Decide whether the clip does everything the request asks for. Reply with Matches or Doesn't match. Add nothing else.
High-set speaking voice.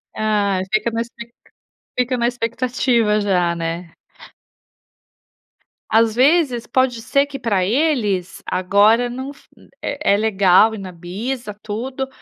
Matches